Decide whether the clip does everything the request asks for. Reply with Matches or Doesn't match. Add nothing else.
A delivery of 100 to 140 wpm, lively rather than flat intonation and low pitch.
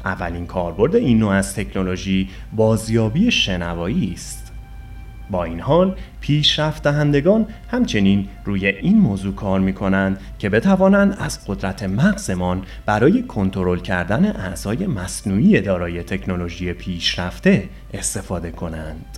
Matches